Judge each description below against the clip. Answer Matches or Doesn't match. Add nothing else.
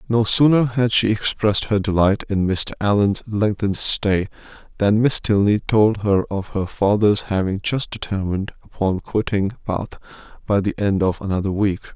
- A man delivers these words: Matches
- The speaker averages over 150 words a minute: Matches